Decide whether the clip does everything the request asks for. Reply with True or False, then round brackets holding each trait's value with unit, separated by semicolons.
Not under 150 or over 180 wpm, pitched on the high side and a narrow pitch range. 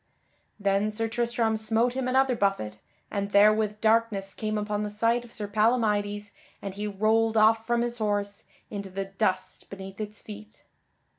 True (160 wpm; 210 Hz; 2.0 semitones)